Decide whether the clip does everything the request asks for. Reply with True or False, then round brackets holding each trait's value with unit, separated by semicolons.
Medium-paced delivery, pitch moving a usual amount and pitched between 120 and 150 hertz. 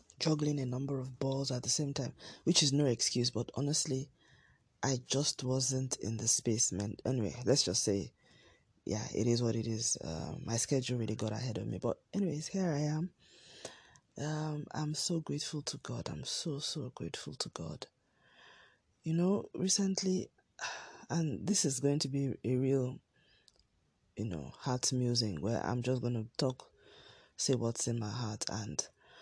True (170 wpm; 4.1 semitones; 135 Hz)